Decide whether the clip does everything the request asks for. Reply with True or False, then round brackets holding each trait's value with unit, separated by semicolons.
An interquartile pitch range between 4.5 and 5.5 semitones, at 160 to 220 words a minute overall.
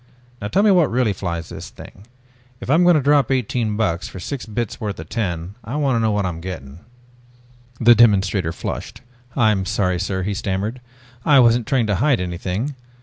True (5.0 semitones; 195 wpm)